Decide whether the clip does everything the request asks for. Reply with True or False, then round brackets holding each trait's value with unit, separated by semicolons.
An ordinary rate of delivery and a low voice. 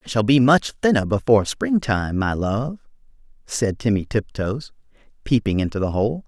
True (155 wpm; 115 Hz)